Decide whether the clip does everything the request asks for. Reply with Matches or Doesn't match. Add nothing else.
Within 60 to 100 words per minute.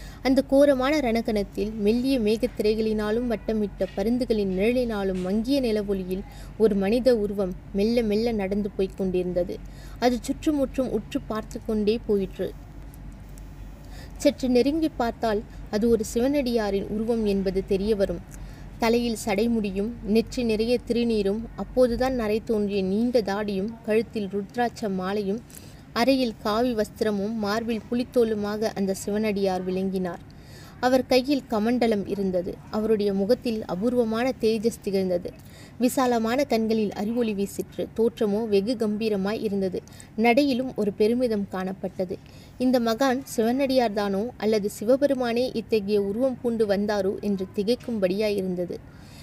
Doesn't match